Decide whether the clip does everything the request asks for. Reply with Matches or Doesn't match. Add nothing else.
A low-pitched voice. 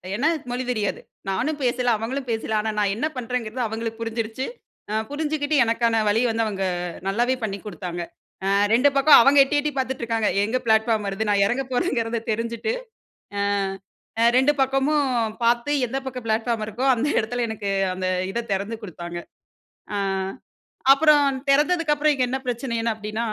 Doesn't match